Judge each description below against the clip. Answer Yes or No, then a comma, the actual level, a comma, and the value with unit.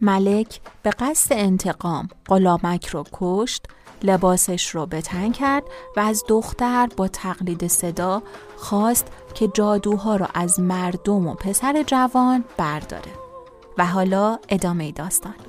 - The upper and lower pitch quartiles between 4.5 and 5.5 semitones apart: No, average, 4.1 semitones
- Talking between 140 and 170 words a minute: No, average, 120 wpm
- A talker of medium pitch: No, high, 195 Hz